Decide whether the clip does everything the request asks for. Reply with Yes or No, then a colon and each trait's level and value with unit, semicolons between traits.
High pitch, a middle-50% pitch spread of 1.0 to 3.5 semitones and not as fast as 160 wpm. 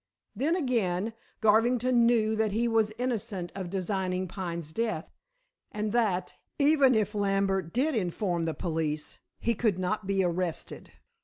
No: high, 205 Hz; average, 4.2 semitones; average, 140 wpm